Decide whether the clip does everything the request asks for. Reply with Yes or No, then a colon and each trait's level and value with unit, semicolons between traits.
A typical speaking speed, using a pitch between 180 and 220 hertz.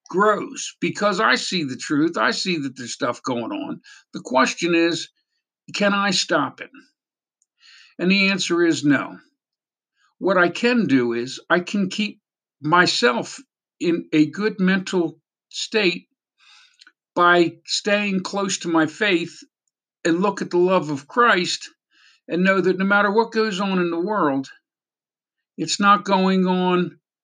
Yes: average, 150 wpm; medium, 185 Hz